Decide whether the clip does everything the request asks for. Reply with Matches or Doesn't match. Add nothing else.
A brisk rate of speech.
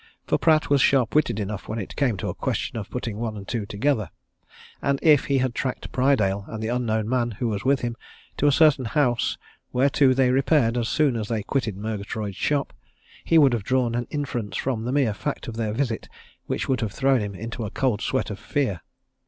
Matches